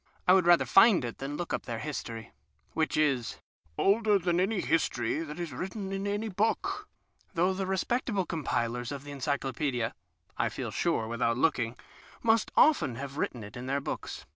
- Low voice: No, medium, 155 Hz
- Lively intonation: Yes, wide, 7.6 semitones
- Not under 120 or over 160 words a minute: No, average, 175 wpm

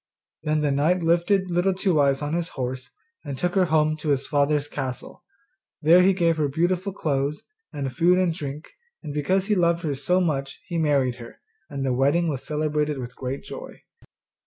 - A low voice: No, medium, 150 Hz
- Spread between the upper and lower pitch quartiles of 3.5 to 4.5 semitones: Yes, average, 3.8 semitones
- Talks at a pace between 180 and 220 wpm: Yes, average, 190 wpm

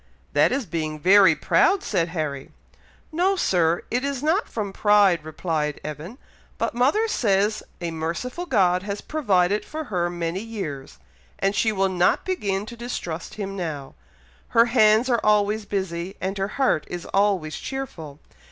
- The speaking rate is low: No, average, 155 wpm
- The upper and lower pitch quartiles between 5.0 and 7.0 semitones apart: Yes, wide, 5.5 semitones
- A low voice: No, high, 195 Hz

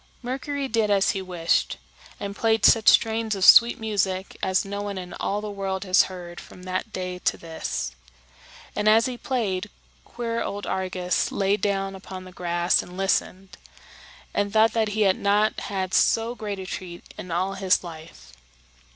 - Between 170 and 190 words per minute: Yes, average, 175 wpm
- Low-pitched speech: No, high, 195 Hz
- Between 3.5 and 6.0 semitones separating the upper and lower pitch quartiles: No, average, 2.8 semitones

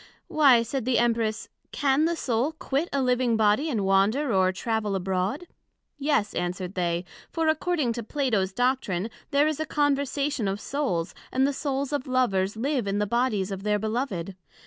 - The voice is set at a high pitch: Yes, high, 240 Hz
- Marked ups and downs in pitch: Yes, wide, 6.0 semitones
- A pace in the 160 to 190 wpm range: Yes, average, 170 wpm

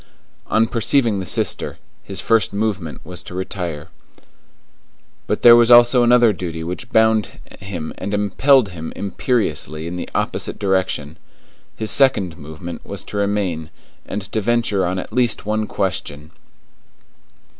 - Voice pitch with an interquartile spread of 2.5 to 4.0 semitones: No, average, 4.4 semitones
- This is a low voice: Yes, low, 100 Hz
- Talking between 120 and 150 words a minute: Yes, average, 140 wpm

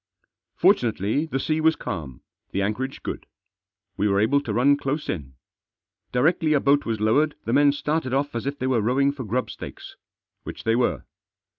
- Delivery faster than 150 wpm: Yes, average, 180 wpm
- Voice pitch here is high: No, low, 130 Hz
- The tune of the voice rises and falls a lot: No, average, 4.7 semitones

